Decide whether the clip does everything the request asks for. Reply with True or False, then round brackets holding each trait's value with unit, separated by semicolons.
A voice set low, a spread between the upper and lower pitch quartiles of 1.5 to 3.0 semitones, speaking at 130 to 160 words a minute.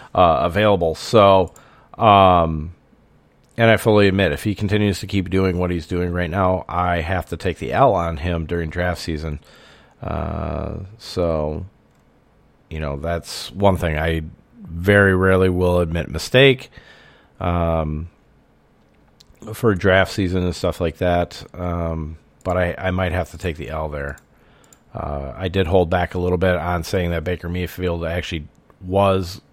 True (90 Hz; 2.5 semitones; 155 wpm)